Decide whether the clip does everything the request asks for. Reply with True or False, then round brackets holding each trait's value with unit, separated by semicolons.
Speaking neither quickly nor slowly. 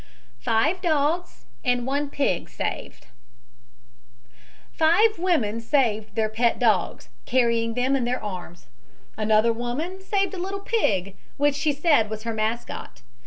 False (130 wpm)